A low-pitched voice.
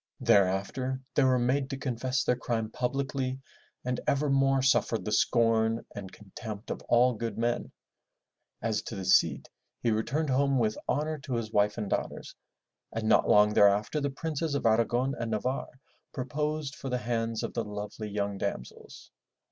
Yes: low, 120 Hz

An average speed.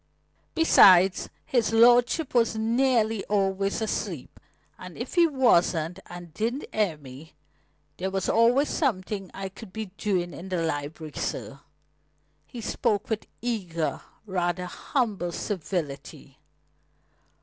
No: slow, 115 wpm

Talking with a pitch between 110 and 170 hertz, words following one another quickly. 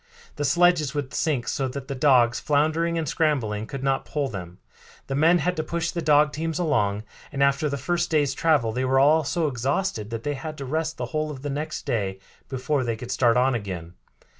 Yes: medium, 140 Hz; fast, 215 wpm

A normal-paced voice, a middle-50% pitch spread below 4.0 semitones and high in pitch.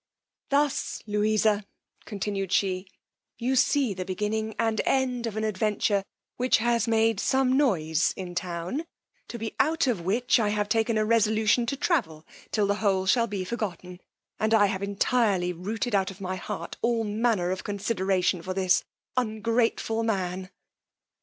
Yes: average, 155 wpm; average, 3.4 semitones; high, 215 Hz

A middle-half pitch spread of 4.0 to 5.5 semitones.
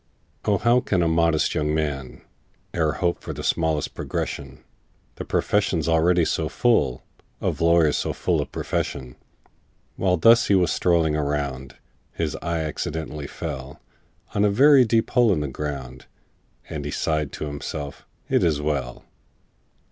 No: average, 3.6 semitones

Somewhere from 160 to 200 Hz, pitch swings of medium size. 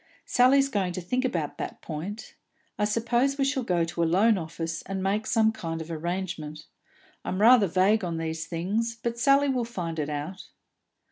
No: high, 190 Hz; wide, 5.8 semitones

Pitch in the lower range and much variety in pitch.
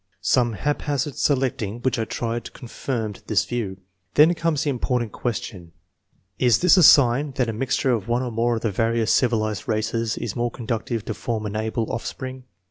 No: low, 120 Hz; average, 2.7 semitones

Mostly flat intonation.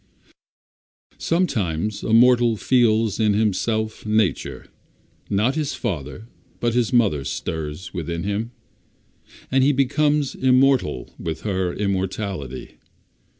No: average, 5.0 semitones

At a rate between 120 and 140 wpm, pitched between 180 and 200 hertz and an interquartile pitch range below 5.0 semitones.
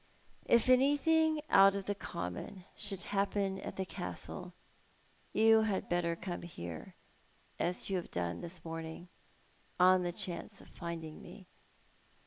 Yes: slow, 135 wpm; medium, 185 Hz; average, 3.1 semitones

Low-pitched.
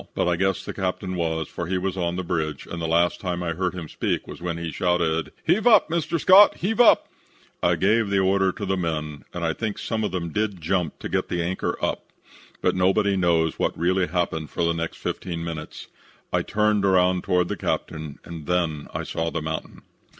Yes: very low, 90 Hz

